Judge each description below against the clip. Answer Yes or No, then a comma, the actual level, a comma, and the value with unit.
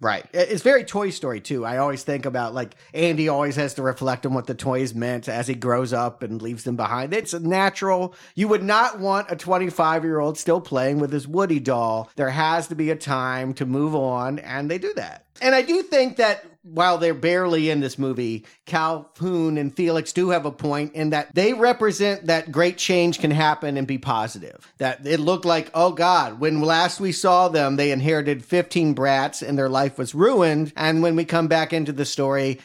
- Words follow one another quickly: Yes, fast, 210 wpm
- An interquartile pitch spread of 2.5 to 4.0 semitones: No, average, 4.6 semitones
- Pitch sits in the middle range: Yes, medium, 155 Hz